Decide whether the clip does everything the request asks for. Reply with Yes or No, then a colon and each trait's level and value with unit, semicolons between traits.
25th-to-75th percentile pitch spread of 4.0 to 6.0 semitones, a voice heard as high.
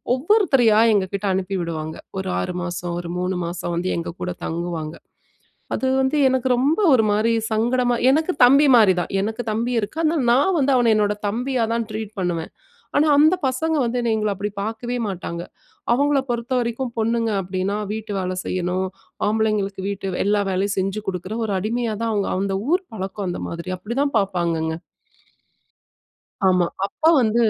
Yes: average, 4.7 semitones; high, 215 Hz